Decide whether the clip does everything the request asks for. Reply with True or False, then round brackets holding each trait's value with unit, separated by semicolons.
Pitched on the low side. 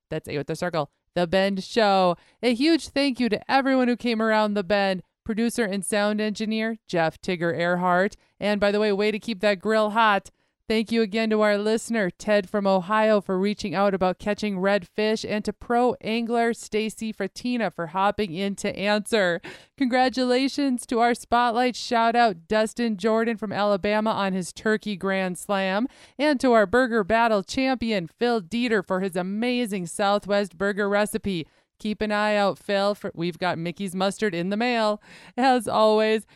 False (210 Hz)